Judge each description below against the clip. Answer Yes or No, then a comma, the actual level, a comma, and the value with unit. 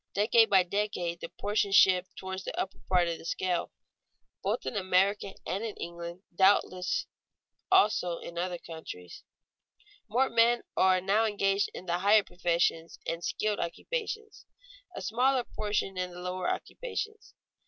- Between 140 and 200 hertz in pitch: Yes, high, 190 Hz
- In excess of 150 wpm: No, average, 145 wpm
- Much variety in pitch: No, average, 3.2 semitones